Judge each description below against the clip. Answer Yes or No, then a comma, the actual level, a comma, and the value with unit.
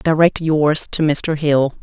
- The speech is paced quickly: No, average, 165 wpm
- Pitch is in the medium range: Yes, medium, 155 Hz